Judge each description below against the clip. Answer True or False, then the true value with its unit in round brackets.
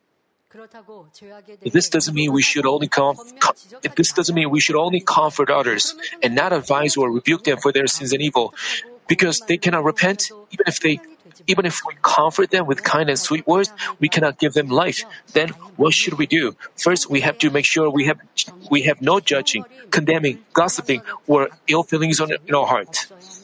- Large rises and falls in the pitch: False (3.8 semitones)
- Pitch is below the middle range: False (155 Hz)